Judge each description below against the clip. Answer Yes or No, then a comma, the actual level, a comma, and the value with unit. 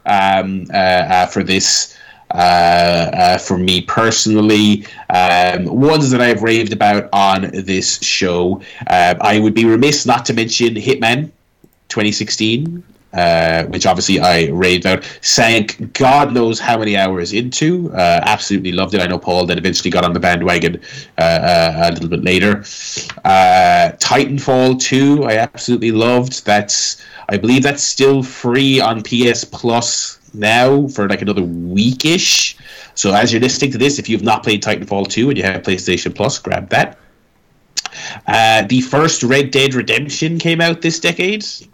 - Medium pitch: No, low, 110 Hz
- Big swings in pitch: Yes, wide, 5.7 semitones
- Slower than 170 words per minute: Yes, average, 160 wpm